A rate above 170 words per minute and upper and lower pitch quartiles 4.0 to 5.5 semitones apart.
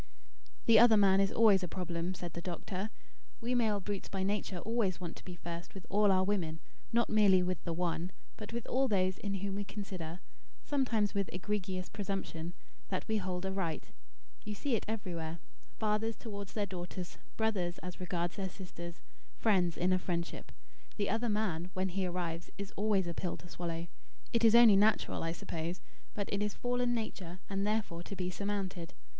No: average, 185 wpm; average, 3.0 semitones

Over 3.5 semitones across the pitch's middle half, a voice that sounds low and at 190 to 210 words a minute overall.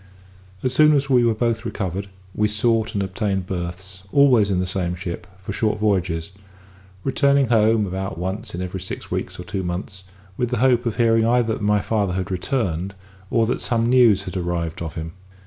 Yes: average, 4.1 semitones; low, 100 Hz; average, 195 wpm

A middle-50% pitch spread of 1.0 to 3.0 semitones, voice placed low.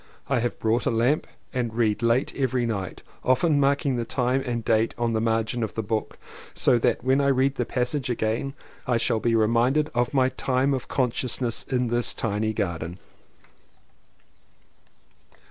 Yes: narrow, 2.6 semitones; low, 120 Hz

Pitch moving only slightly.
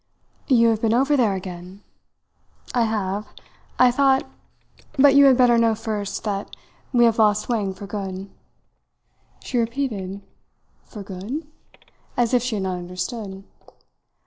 No: average, 3.9 semitones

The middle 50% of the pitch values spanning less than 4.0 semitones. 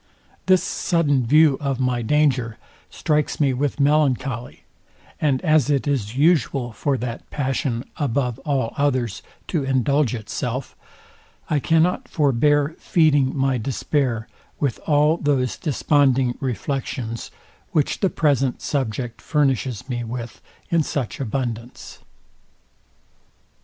Yes: average, 3.1 semitones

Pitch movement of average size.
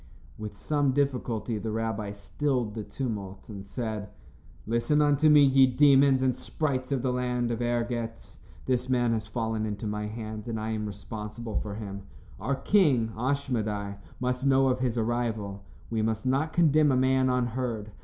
Yes: average, 3.4 semitones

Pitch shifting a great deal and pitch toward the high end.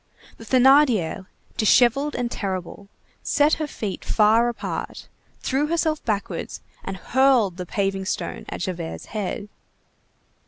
Yes: wide, 5.7 semitones; high, 220 Hz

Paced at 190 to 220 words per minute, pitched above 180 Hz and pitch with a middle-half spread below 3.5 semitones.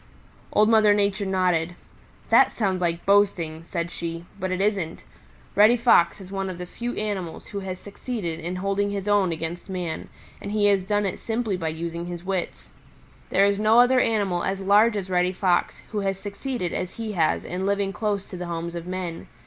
Yes: average, 195 wpm; high, 190 Hz; average, 2.8 semitones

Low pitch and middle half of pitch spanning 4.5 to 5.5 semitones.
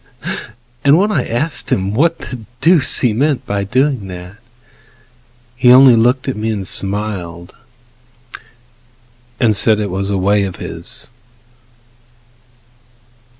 Yes: low, 110 Hz; average, 5.1 semitones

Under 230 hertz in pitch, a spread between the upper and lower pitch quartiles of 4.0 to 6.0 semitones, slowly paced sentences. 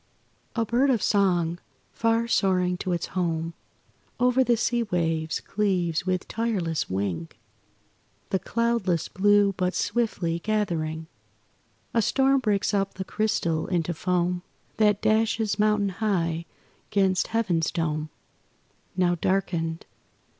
Yes: high, 190 Hz; average, 4.4 semitones; slow, 120 wpm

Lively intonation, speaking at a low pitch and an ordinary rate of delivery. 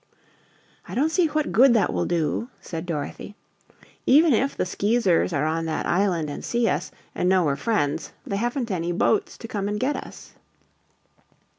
No: wide, 6.5 semitones; high, 200 Hz; average, 175 wpm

